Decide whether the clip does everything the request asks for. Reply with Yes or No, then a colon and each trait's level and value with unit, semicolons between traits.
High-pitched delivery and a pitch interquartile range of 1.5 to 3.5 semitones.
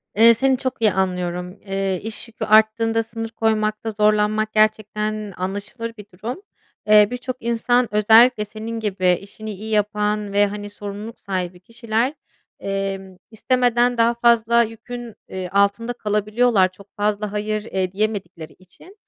Yes: high, 215 Hz; narrow, 2.4 semitones